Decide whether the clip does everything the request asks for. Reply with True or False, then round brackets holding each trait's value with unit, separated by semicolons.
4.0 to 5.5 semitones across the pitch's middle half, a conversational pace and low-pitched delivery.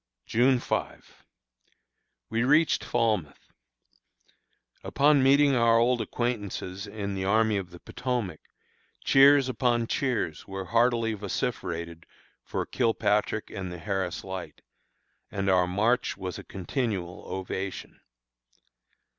False (4.6 semitones; 110 wpm; 110 Hz)